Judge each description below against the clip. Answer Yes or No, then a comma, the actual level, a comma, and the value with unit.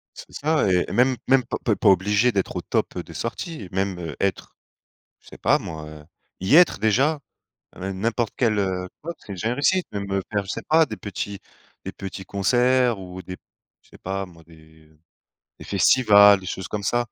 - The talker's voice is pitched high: No, low, 100 Hz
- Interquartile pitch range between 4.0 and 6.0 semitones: Yes, average, 4.6 semitones